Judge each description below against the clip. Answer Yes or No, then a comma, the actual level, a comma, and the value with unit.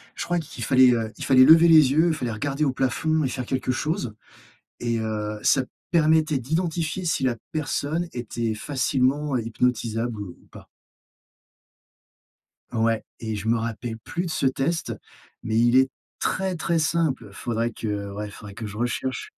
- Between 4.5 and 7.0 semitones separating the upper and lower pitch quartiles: Yes, wide, 5.5 semitones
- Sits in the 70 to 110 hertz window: No, low, 130 Hz